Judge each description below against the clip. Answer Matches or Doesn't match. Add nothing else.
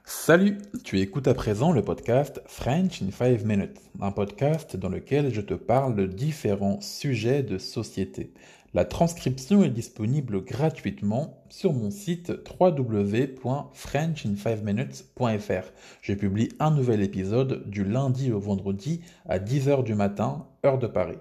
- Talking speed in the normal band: Doesn't match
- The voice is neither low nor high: Doesn't match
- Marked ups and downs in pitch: Matches